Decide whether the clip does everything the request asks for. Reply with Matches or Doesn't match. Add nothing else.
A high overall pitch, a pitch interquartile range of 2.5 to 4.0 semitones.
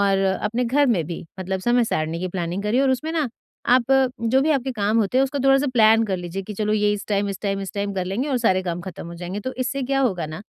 Doesn't match